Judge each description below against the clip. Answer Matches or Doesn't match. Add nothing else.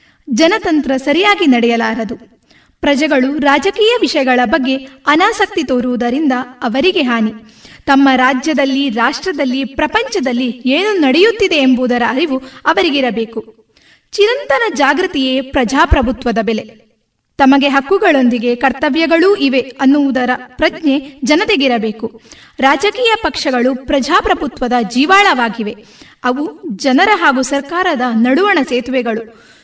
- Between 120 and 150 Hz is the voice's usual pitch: Doesn't match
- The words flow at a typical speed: Matches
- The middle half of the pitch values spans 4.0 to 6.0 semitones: Matches